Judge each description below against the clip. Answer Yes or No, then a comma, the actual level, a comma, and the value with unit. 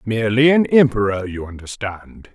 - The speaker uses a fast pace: No, slow, 130 wpm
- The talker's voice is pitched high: No, low, 110 Hz